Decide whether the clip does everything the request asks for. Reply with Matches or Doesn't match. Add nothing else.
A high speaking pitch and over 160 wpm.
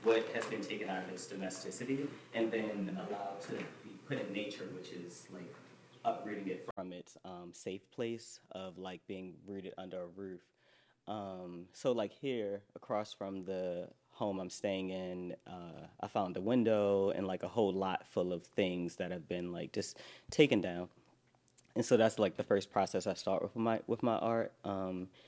Doesn't match